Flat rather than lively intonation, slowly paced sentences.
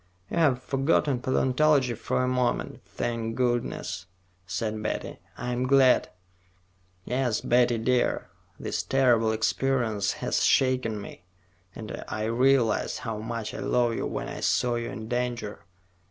Yes: narrow, 2.3 semitones; slow, 130 wpm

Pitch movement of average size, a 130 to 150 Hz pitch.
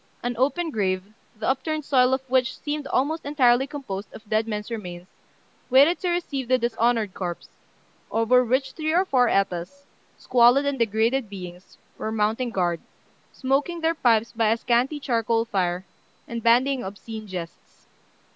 No: average, 4.1 semitones; high, 240 Hz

